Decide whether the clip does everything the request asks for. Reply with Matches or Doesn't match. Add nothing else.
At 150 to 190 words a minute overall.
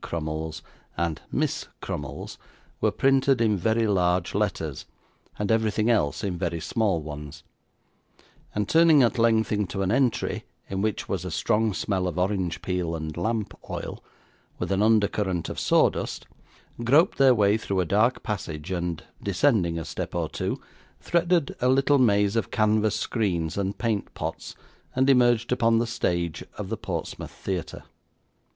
Matches